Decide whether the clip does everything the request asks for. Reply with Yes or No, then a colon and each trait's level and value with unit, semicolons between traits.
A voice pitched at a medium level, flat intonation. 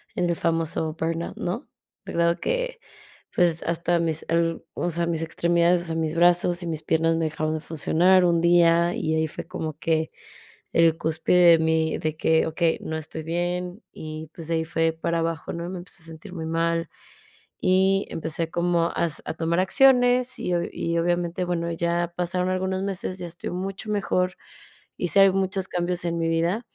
Yes: medium, 170 Hz; narrow, 1.6 semitones